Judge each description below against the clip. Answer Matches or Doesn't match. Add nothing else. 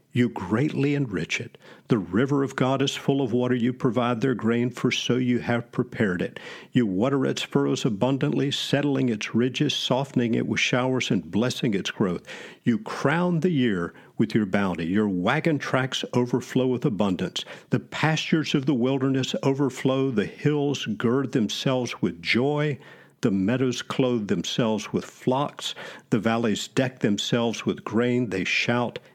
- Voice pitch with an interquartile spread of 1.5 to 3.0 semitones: Matches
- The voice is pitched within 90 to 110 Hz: Doesn't match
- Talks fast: Doesn't match